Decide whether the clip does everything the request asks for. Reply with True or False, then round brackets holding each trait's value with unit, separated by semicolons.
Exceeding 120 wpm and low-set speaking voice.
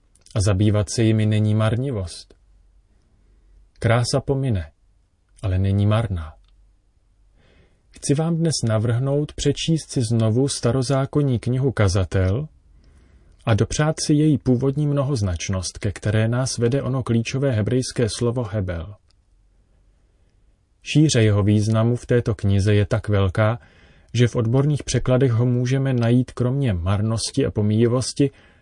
False (115 wpm; 110 Hz)